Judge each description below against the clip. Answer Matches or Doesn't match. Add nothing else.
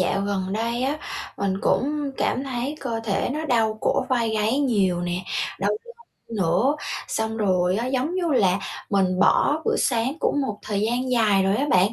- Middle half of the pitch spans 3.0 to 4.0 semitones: Doesn't match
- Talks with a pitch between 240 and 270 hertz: Doesn't match